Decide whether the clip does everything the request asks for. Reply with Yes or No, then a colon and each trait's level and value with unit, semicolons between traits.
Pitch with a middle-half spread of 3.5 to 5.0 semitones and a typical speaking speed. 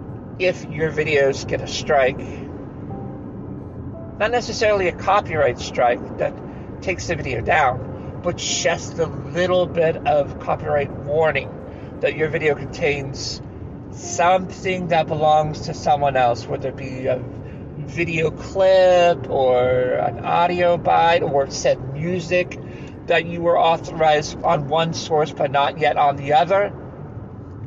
No: average, 3.9 semitones; slow, 130 wpm